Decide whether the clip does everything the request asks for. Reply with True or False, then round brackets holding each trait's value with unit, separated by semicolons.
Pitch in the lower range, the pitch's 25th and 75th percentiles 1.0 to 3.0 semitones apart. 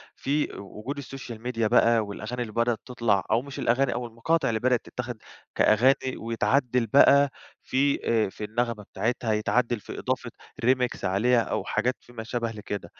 True (120 Hz; 2.4 semitones)